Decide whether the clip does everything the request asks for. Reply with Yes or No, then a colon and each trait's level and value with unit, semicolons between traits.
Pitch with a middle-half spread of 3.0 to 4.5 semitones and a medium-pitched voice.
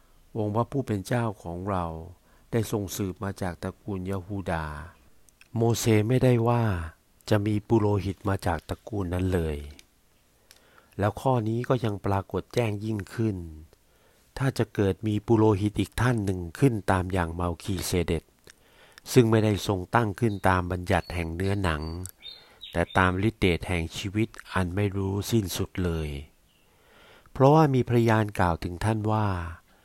No: average, 3.7 semitones; low, 100 Hz